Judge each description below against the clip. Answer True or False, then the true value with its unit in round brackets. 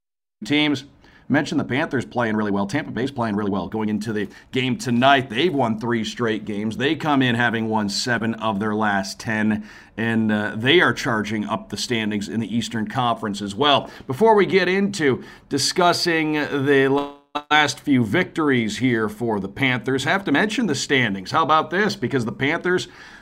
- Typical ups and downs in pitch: True (4.9 semitones)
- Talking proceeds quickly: False (185 wpm)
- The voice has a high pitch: False (120 Hz)